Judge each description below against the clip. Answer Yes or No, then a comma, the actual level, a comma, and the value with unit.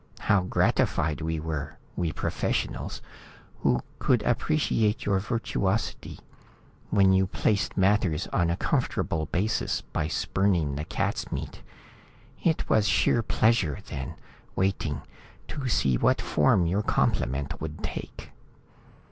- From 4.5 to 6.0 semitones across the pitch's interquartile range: Yes, average, 5.1 semitones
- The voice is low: Yes, very low, 95 Hz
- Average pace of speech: No, slow, 120 wpm